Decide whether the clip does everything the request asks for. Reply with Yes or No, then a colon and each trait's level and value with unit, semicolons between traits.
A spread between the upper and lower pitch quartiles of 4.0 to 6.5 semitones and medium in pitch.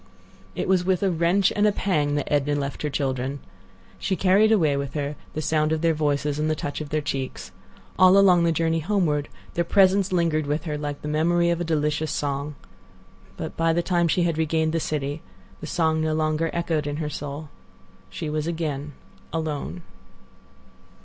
No: narrow, 2.6 semitones; medium, 155 Hz